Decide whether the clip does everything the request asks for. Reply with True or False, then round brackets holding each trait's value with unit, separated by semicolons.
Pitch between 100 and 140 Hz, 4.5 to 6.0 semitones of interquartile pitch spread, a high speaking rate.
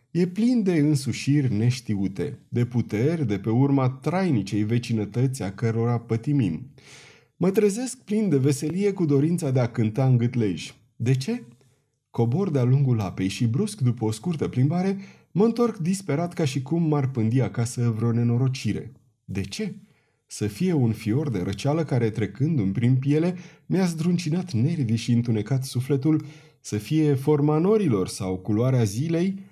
False (135 Hz; 5.1 semitones; 155 wpm)